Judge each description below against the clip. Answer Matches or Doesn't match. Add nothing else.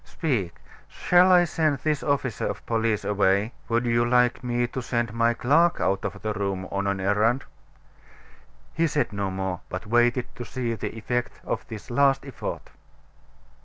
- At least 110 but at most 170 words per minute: Matches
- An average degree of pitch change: Matches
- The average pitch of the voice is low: Matches